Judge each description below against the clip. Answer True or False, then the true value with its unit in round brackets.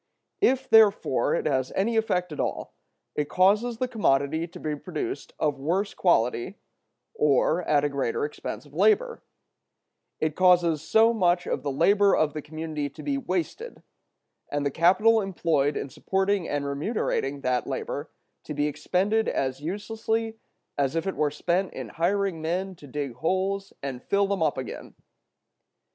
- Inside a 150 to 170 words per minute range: True (160 wpm)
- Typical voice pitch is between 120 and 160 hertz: False (170 Hz)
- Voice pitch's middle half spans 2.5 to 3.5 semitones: False (5.5 semitones)